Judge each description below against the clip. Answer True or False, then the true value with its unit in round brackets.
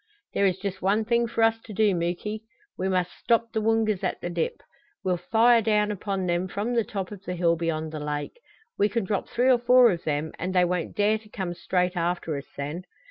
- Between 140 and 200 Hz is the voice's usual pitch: True (190 Hz)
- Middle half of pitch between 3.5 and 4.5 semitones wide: True (4.0 semitones)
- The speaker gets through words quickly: True (230 wpm)